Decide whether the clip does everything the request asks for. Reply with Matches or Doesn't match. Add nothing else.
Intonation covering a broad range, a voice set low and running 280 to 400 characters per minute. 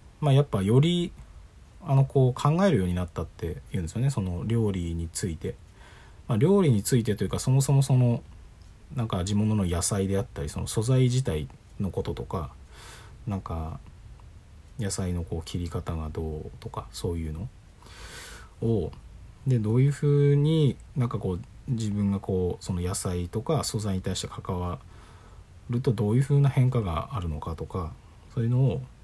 Matches